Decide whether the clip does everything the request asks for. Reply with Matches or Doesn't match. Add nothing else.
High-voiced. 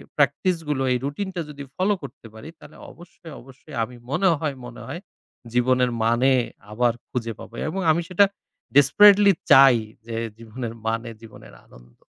Doesn't match